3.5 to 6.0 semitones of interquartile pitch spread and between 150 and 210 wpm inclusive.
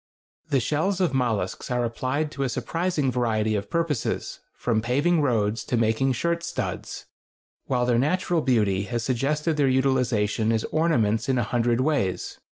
Yes: average, 4.8 semitones; average, 155 wpm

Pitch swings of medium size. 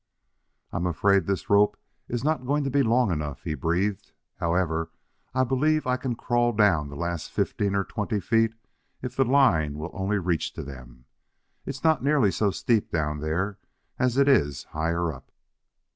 No: wide, 7.4 semitones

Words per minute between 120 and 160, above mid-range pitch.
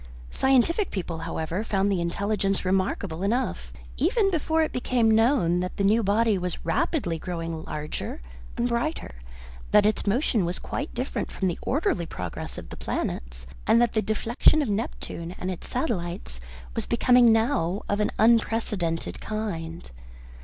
Yes: average, 155 wpm; high, 205 Hz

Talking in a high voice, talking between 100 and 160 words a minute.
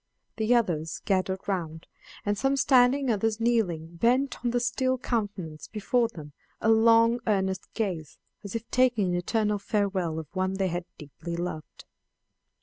Yes: high, 205 Hz; average, 150 wpm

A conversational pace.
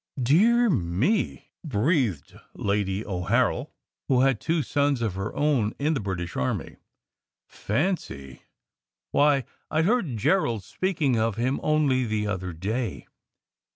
No: slow, 125 wpm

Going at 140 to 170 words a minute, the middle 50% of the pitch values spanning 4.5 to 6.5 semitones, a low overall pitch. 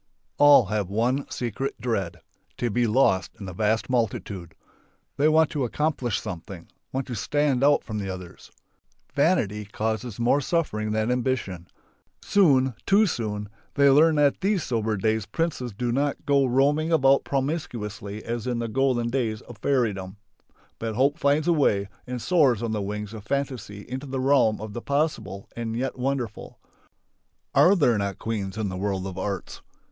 Yes: average, 165 wpm; average, 4.9 semitones; low, 120 Hz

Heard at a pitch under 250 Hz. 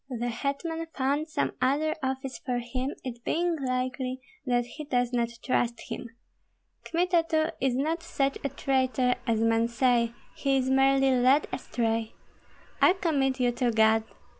No: very high, 260 Hz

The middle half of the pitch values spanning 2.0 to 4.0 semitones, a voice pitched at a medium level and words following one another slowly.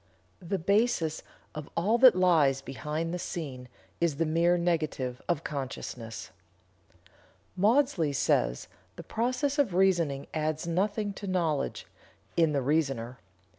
No: average, 5.1 semitones; medium, 165 Hz; slow, 125 wpm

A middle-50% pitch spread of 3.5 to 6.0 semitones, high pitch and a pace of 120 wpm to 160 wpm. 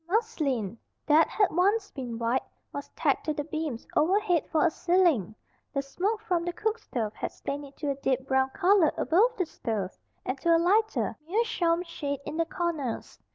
No: wide, 5.4 semitones; very high, 320 Hz; average, 180 wpm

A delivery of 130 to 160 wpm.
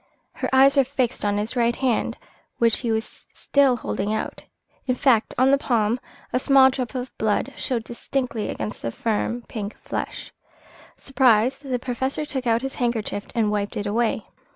No: average, 175 wpm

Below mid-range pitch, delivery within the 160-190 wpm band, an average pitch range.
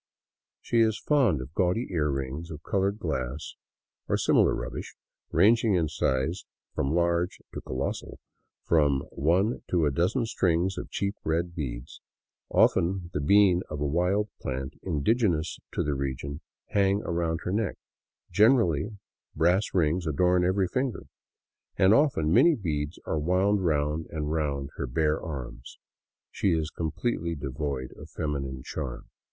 No: very low, 85 Hz; average, 140 wpm; average, 4.7 semitones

